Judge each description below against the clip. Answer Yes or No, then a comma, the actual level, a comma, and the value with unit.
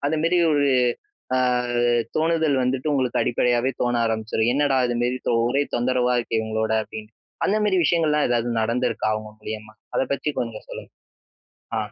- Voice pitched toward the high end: No, low, 125 Hz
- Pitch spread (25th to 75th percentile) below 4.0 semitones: No, average, 4.4 semitones